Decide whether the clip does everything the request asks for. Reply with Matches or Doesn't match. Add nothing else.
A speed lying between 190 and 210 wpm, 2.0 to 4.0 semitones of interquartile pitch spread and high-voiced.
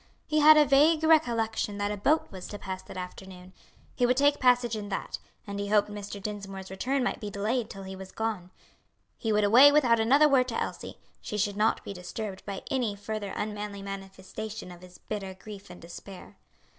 Matches